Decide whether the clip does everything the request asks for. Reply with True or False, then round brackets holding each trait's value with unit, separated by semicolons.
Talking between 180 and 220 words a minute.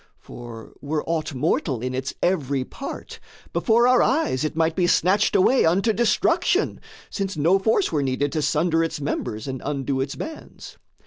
False (170 wpm)